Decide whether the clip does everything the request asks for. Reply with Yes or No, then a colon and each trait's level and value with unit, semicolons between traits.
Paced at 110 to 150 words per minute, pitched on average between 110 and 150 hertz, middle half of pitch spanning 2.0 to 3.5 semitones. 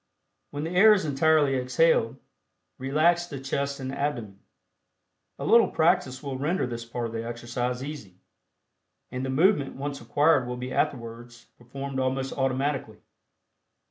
Yes: average, 140 wpm; low, 135 Hz; average, 3.1 semitones